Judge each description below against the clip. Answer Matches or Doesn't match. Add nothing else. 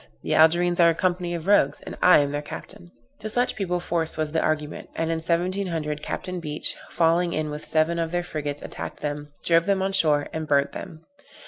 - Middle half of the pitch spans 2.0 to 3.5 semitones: Matches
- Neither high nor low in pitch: Matches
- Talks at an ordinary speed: Doesn't match